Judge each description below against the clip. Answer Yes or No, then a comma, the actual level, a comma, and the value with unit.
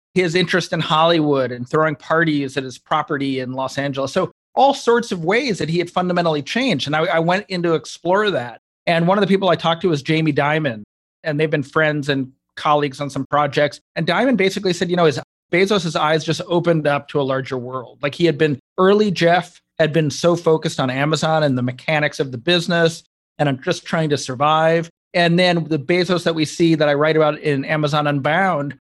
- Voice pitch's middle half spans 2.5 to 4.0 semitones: Yes, average, 3.3 semitones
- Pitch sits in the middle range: Yes, medium, 160 Hz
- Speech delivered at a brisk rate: Yes, fast, 220 wpm